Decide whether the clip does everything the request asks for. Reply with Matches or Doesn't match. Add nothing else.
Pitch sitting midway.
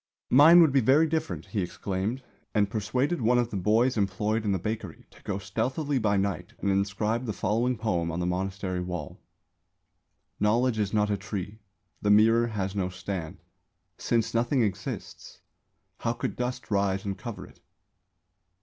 Doesn't match